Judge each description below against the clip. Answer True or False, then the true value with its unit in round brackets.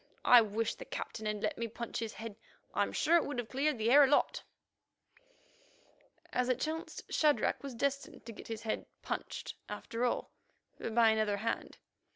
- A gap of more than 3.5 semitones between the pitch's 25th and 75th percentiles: True (3.9 semitones)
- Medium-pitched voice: False (235 Hz)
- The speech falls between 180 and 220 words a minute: True (185 wpm)